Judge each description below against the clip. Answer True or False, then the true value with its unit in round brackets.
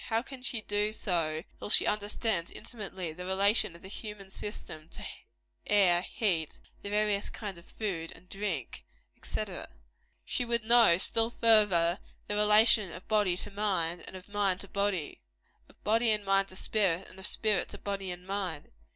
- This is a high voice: True (200 Hz)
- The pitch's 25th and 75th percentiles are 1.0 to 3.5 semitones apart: True (2.8 semitones)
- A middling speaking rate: True (170 wpm)